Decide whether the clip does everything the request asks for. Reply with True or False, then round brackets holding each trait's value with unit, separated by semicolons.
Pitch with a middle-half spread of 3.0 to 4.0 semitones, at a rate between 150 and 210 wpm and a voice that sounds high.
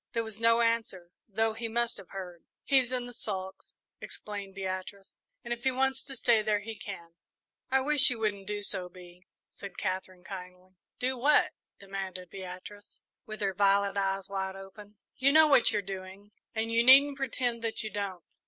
True (3.6 semitones; 180 wpm; 205 Hz)